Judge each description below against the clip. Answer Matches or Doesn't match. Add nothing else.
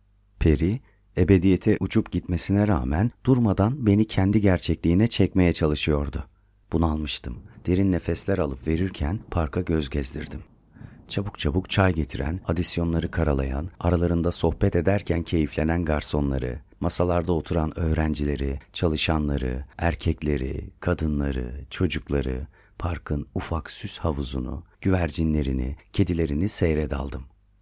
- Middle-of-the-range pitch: Doesn't match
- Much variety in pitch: Doesn't match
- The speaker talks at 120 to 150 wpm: Doesn't match